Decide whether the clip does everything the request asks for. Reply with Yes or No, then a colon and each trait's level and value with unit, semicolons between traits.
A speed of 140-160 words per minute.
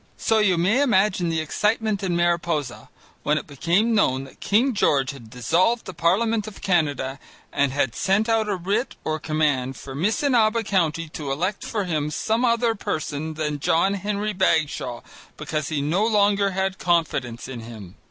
No: average, 170 wpm